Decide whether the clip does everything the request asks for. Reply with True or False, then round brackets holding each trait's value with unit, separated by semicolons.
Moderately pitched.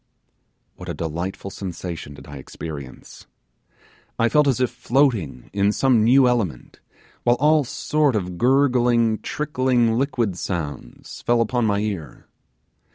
False (115 Hz)